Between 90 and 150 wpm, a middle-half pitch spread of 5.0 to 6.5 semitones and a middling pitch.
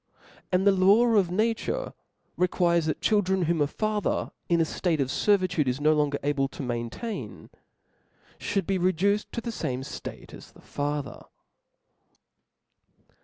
Yes: average, 145 wpm; wide, 5.5 semitones; medium, 180 Hz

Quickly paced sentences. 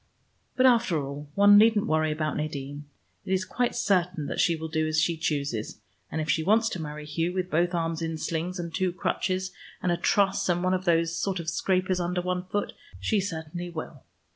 Yes: fast, 210 wpm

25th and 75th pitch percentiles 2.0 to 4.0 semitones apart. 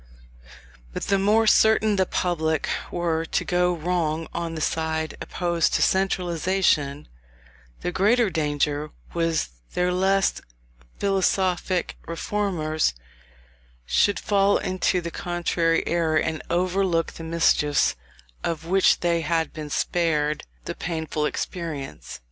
Yes: average, 2.8 semitones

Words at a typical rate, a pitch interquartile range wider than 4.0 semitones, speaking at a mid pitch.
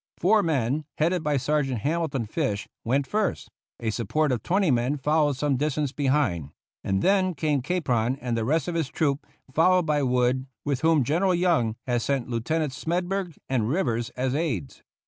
Yes: average, 170 wpm; average, 4.7 semitones; medium, 145 Hz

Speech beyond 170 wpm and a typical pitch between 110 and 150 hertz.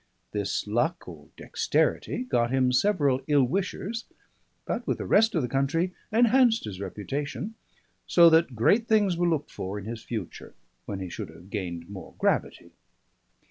No: average, 160 wpm; low, 135 Hz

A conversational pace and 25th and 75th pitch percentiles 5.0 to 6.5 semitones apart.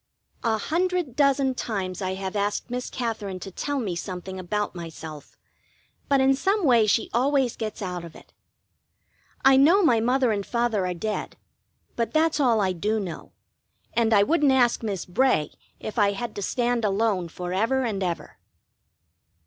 Yes: average, 170 wpm; wide, 5.4 semitones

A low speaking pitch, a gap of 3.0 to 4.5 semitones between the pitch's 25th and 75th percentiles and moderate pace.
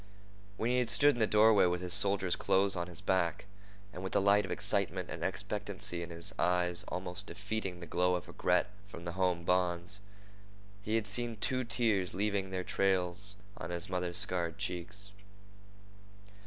No: very low, 95 Hz; narrow, 2.6 semitones; average, 175 wpm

